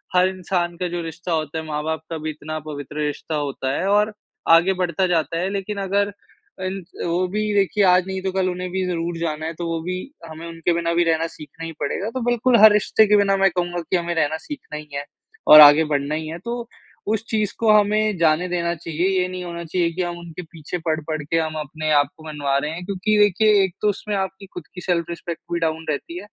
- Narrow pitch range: No, average, 3.3 semitones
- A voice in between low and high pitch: Yes, medium, 175 Hz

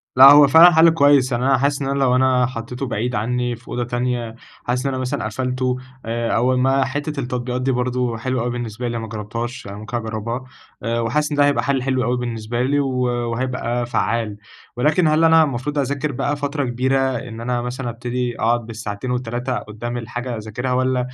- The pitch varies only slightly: Yes, narrow, 2.3 semitones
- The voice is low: Yes, low, 125 Hz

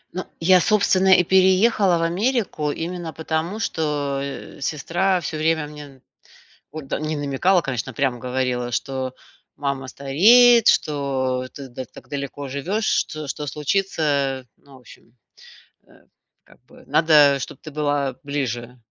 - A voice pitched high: No, medium, 150 Hz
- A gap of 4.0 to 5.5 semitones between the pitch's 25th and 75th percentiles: Yes, average, 4.5 semitones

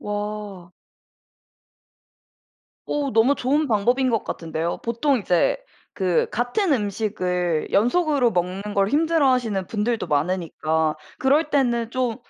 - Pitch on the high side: Yes, high, 220 Hz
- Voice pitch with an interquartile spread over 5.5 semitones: Yes, wide, 5.9 semitones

